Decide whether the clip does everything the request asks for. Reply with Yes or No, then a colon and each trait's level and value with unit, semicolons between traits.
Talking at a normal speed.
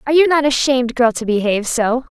No: fast, 225 wpm